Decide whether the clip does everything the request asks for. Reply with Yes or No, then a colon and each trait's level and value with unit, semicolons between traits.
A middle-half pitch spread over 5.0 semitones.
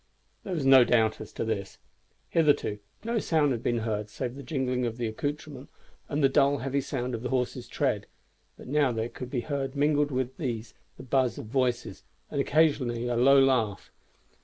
No: average, 3.0 semitones